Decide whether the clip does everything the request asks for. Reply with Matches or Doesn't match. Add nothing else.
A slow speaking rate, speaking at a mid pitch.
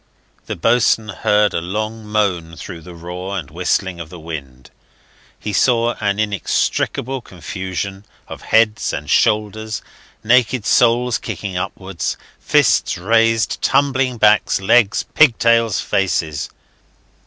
Doesn't match